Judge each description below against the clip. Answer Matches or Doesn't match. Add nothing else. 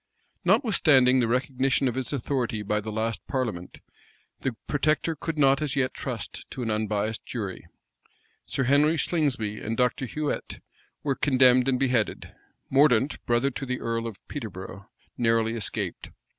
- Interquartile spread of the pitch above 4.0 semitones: Doesn't match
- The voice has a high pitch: Doesn't match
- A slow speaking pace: Doesn't match